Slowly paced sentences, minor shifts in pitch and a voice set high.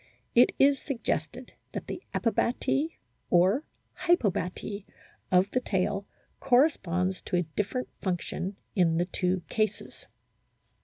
No: slow, 120 wpm; wide, 5.6 semitones; high, 200 Hz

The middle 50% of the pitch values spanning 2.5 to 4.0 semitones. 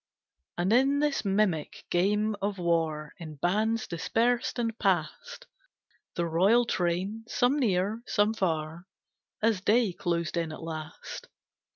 No: average, 4.9 semitones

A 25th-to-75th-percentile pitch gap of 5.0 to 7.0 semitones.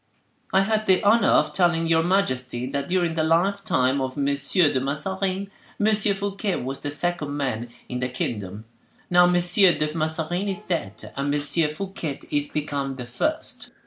Yes: wide, 5.4 semitones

